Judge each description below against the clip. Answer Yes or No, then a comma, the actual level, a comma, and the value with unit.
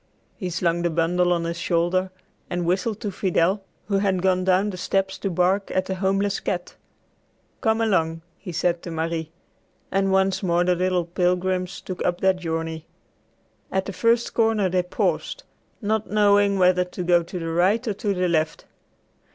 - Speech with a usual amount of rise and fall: No, narrow, 2.0 semitones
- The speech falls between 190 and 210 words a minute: No, average, 175 wpm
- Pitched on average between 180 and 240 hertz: Yes, medium, 185 Hz